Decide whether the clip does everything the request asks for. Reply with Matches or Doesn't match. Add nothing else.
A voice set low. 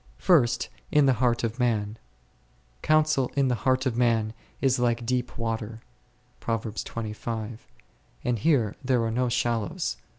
Matches